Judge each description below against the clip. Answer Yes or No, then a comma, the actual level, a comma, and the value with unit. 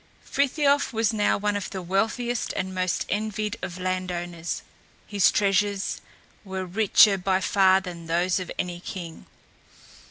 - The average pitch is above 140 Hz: Yes, high, 190 Hz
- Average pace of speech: Yes, average, 145 wpm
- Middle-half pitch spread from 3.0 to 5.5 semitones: No, narrow, 2.4 semitones